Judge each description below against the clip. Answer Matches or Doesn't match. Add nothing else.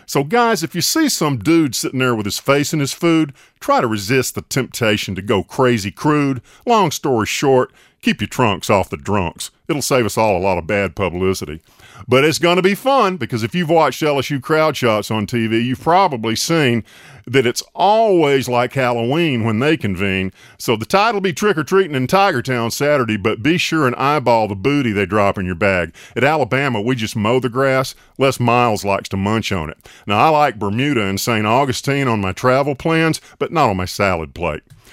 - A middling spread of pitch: Doesn't match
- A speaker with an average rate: Doesn't match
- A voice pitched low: Matches